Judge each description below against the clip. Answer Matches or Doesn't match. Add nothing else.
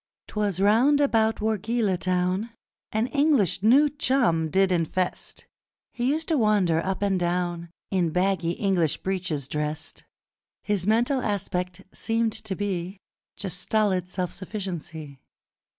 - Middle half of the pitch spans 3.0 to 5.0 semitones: Matches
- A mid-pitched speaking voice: Doesn't match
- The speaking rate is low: Matches